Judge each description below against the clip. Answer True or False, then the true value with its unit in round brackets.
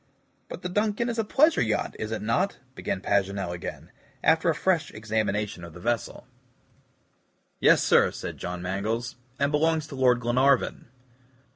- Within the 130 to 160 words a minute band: True (155 wpm)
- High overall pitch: False (120 Hz)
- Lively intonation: True (7.9 semitones)